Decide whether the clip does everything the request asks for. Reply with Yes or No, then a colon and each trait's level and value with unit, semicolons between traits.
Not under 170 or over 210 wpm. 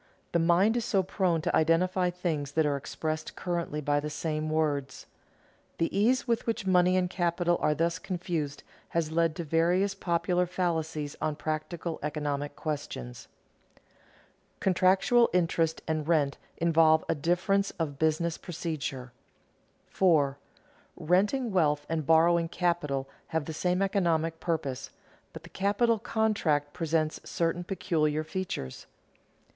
No: slow, 135 wpm